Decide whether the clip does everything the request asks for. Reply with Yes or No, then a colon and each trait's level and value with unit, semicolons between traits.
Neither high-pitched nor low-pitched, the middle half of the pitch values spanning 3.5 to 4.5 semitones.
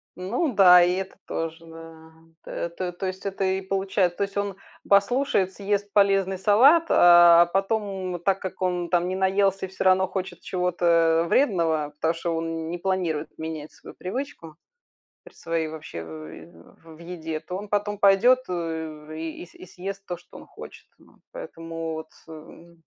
No: medium, 180 Hz; average, 3.0 semitones